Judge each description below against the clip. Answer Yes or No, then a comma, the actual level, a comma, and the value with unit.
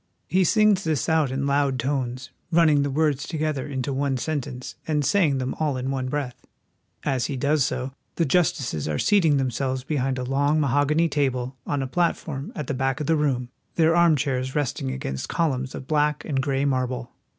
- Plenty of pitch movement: No, average, 2.9 semitones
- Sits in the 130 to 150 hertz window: Yes, medium, 140 Hz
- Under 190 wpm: No, average, 195 wpm